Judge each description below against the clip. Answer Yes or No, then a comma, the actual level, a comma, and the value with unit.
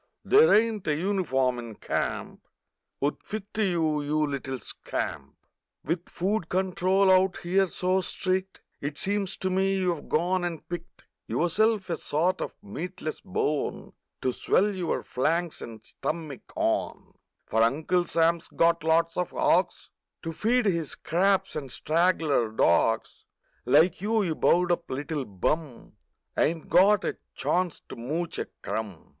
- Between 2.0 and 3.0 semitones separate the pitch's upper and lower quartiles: No, average, 4.0 semitones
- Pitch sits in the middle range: Yes, medium, 170 Hz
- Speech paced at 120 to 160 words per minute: Yes, average, 150 wpm